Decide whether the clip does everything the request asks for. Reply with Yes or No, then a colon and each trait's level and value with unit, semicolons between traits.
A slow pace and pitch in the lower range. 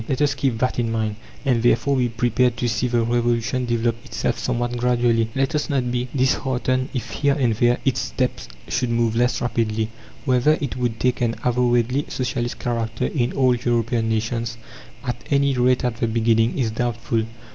No: average, 180 wpm; low, 120 Hz